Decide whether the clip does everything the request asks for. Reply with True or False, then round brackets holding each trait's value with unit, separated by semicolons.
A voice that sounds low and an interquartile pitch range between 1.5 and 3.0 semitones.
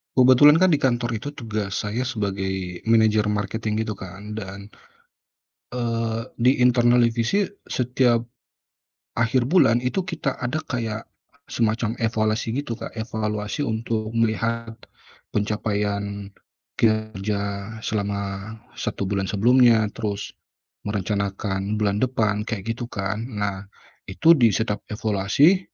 True (110 Hz; 2.6 semitones)